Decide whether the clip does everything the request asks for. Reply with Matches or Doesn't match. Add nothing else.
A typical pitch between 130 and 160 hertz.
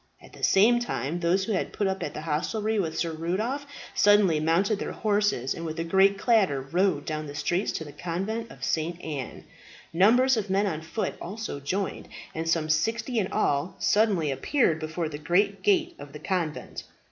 Doesn't match